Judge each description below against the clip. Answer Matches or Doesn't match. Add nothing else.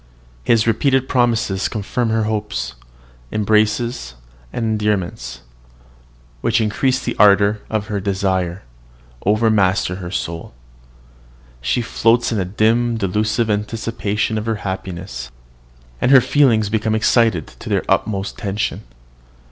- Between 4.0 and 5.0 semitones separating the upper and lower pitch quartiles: Doesn't match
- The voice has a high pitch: Doesn't match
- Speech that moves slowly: Matches